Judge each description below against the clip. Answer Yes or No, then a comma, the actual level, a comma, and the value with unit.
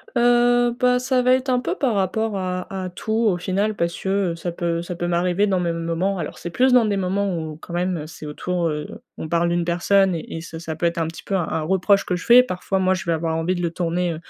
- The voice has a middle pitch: Yes, medium, 180 Hz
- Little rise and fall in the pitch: No, average, 3.0 semitones